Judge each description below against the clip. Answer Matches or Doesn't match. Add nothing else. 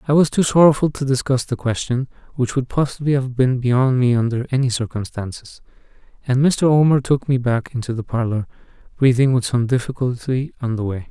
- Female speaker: Doesn't match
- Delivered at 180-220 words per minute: Matches